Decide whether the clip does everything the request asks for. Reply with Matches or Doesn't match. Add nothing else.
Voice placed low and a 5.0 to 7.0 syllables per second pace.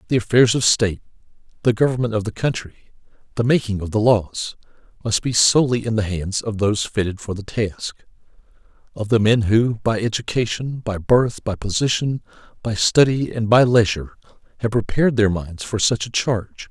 Matches